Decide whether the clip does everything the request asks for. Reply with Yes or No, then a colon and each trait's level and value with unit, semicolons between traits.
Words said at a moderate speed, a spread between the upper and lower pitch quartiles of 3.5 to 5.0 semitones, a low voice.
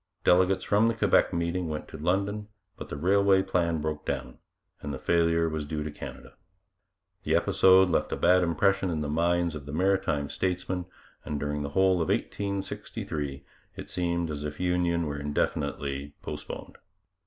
Yes: average, 165 wpm; average, 3.8 semitones; very low, 85 Hz